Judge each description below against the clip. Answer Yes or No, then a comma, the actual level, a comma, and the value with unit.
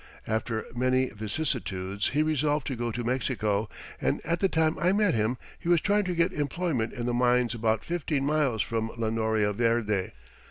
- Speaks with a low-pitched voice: Yes, low, 125 Hz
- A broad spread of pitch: Yes, wide, 5.7 semitones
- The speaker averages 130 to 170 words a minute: No, average, 185 wpm